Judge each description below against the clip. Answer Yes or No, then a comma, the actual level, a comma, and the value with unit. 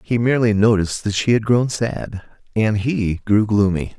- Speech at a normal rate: Yes, average, 180 wpm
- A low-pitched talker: Yes, low, 105 Hz